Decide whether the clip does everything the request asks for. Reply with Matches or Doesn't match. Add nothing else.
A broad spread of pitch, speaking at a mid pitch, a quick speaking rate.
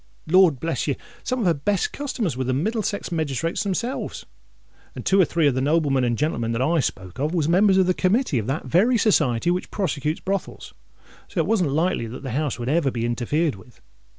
Matches